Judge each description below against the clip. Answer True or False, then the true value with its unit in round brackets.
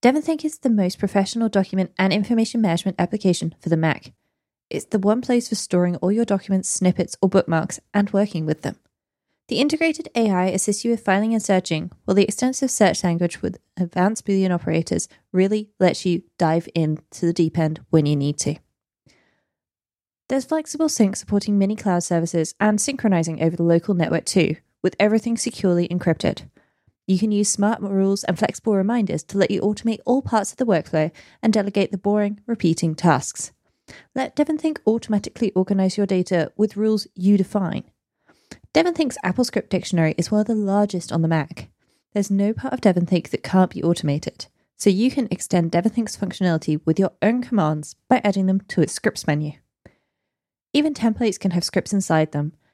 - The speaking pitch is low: False (195 Hz)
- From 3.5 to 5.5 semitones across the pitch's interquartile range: True (4.0 semitones)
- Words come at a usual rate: True (175 wpm)